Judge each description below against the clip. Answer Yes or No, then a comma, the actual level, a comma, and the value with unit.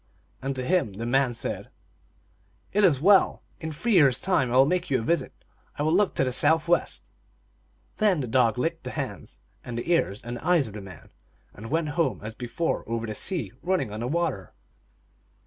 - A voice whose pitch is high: No, low, 135 Hz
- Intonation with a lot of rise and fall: Yes, wide, 6.5 semitones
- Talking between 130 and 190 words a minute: No, fast, 205 wpm